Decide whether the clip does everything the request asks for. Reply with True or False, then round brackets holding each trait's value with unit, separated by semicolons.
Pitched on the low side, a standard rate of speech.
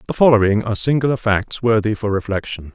True (110 Hz; 175 wpm)